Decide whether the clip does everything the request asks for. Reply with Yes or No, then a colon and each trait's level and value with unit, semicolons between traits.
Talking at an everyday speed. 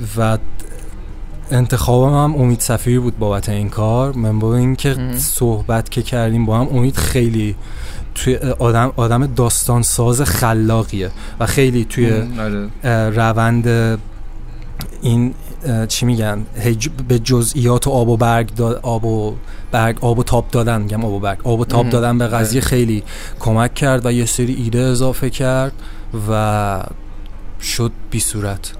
Yes: average, 145 wpm